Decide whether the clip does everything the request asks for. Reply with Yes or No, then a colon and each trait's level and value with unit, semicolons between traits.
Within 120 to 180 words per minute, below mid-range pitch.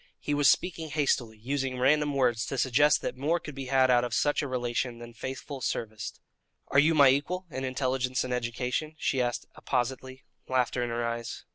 No: average, 190 wpm; low, 130 Hz